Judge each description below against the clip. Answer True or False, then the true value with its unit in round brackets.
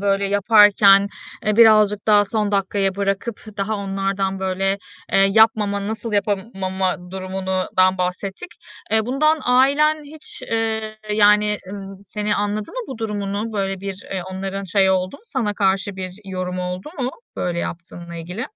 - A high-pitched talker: True (200 Hz)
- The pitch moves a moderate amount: False (2.2 semitones)